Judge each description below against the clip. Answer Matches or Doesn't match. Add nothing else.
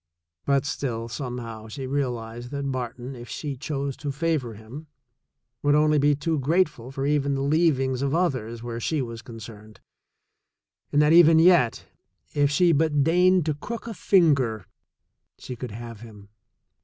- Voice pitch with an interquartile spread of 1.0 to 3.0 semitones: Doesn't match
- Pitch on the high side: Doesn't match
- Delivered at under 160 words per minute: Doesn't match